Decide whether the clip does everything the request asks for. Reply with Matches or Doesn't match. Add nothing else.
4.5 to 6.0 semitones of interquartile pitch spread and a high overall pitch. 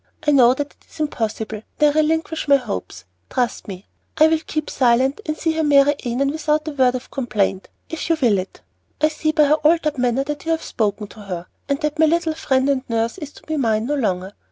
Matches